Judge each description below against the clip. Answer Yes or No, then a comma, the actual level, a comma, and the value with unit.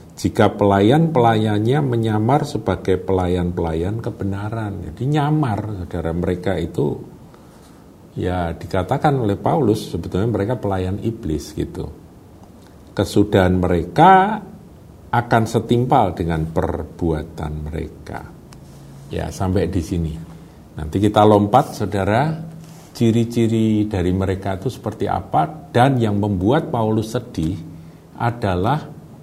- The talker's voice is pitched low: Yes, low, 105 Hz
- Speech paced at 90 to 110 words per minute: Yes, average, 95 wpm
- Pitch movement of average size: Yes, average, 4.8 semitones